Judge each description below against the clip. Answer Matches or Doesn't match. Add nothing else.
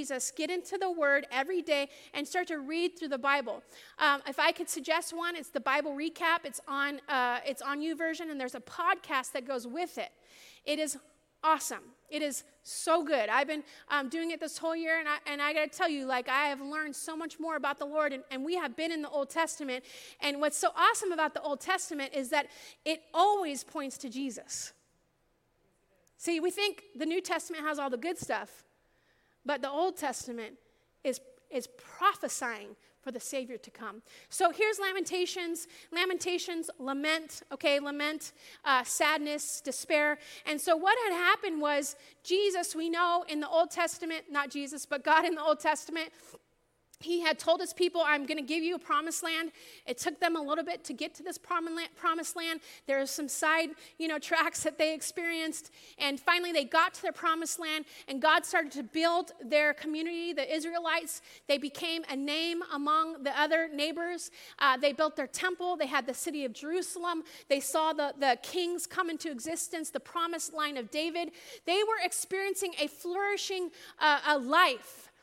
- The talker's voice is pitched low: Doesn't match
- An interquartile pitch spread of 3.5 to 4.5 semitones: Doesn't match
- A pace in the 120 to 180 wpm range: Doesn't match